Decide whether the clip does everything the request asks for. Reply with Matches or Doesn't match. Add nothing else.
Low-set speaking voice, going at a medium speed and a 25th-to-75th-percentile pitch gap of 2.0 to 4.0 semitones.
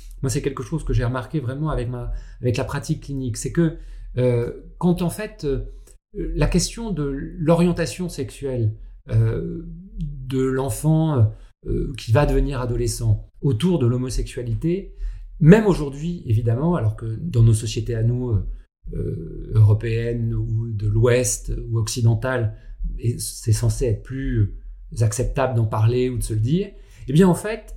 Doesn't match